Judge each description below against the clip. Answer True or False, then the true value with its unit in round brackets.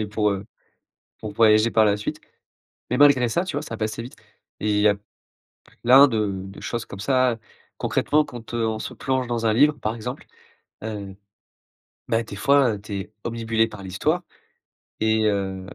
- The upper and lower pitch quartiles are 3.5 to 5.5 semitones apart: False (2.9 semitones)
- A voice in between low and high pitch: False (110 Hz)